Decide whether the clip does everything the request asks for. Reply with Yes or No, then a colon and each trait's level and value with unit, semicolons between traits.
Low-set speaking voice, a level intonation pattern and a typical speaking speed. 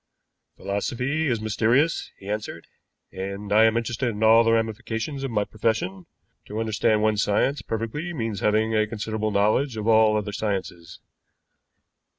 Yes: low, 110 Hz; narrow, 1.8 semitones; average, 150 wpm